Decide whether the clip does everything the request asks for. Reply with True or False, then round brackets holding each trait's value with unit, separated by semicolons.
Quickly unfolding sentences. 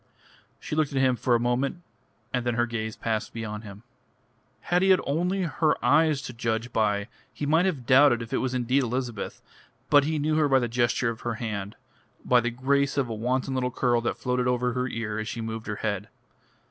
True (215 wpm)